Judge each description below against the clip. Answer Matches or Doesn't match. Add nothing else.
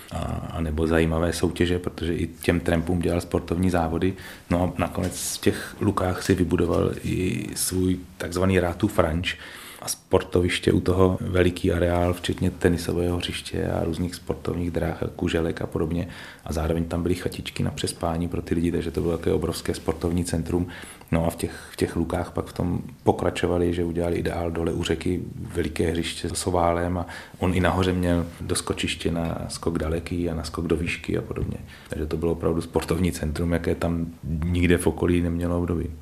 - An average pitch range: Doesn't match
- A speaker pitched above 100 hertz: Doesn't match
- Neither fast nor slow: Doesn't match